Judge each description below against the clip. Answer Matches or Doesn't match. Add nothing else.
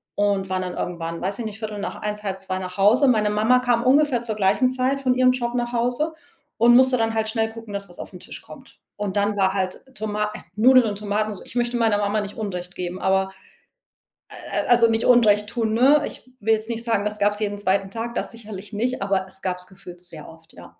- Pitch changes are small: Doesn't match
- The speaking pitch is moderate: Doesn't match